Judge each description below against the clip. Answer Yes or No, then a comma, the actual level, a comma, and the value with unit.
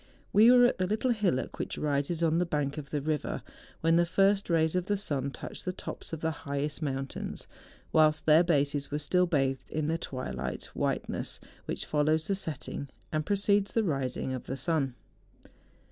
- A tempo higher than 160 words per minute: Yes, average, 190 wpm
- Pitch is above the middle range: No, medium, 155 Hz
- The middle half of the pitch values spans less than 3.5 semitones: No, average, 4.2 semitones